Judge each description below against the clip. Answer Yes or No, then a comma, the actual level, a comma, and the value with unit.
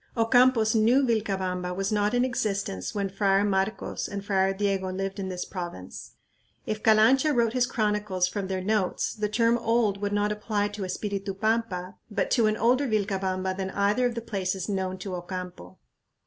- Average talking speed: Yes, average, 175 wpm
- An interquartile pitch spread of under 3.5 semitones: Yes, narrow, 2.6 semitones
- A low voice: No, high, 205 Hz